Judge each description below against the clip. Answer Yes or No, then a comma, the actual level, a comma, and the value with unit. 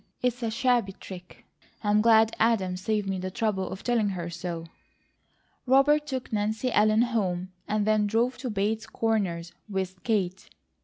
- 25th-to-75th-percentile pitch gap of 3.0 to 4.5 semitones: Yes, average, 3.4 semitones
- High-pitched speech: Yes, high, 215 Hz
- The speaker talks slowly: No, average, 155 wpm